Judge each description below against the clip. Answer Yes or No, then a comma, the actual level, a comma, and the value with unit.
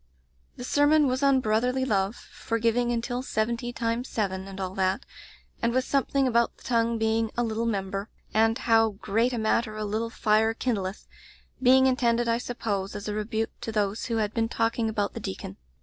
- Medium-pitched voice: No, high, 225 Hz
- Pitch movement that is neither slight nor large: No, narrow, 2.3 semitones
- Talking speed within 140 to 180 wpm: No, average, 200 wpm